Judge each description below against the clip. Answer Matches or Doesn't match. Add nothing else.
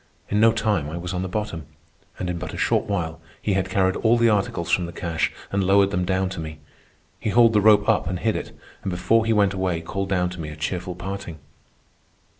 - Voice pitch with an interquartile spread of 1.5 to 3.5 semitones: Matches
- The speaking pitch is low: Matches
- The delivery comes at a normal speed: Doesn't match